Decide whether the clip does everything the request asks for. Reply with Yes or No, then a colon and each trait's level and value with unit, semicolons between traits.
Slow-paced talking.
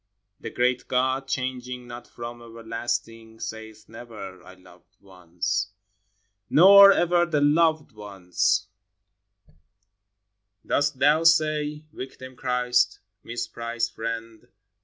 Yes: slow, 100 wpm